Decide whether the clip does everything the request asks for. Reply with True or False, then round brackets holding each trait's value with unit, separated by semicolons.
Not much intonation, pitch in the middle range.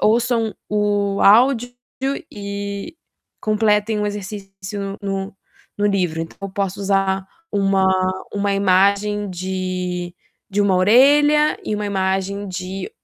False (1.5 semitones; 200 Hz)